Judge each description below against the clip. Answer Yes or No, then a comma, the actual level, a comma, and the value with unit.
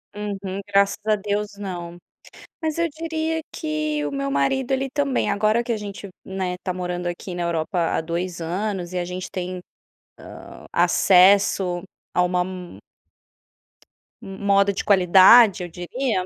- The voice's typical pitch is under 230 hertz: Yes, high, 190 Hz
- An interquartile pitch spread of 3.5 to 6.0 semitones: No, average, 2.9 semitones